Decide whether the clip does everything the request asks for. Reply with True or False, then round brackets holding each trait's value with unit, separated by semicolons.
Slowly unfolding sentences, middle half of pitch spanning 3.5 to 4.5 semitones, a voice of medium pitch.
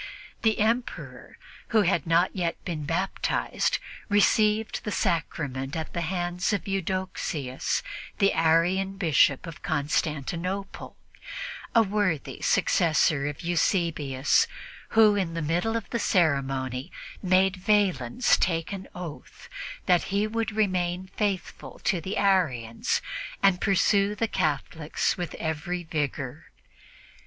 True (115 wpm; 4.0 semitones; 175 Hz)